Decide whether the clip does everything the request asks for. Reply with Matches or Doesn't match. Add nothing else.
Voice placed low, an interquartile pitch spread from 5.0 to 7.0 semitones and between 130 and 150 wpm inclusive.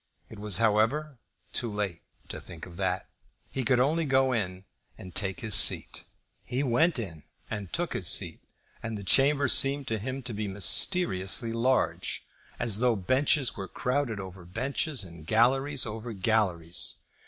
Doesn't match